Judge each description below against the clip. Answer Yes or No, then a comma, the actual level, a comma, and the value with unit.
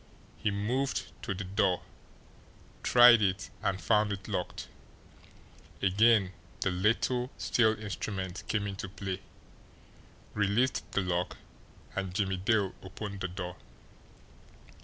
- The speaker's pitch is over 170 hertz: No, low, 100 Hz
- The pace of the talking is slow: Yes, slow, 115 wpm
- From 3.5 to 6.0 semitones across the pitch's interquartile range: No, narrow, 2.4 semitones